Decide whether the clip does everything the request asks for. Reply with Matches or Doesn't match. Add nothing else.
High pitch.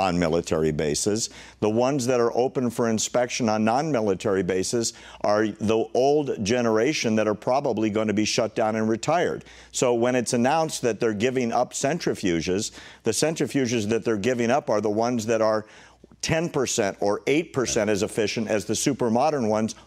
Doesn't match